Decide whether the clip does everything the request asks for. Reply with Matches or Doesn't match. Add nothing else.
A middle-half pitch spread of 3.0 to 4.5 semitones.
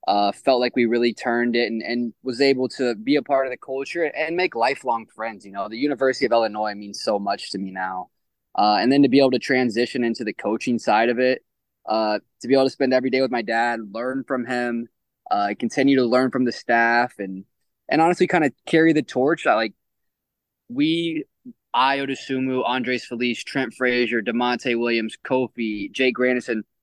Doesn't match